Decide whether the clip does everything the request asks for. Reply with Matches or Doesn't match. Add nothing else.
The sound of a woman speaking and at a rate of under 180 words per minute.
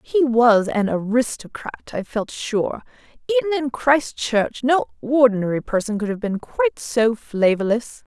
Matches